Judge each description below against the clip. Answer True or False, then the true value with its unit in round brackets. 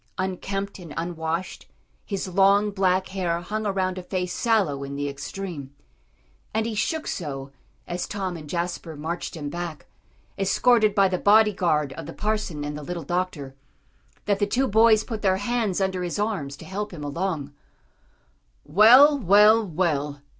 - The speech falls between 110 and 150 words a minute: False (160 wpm)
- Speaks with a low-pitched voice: False (185 Hz)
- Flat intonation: False (4.4 semitones)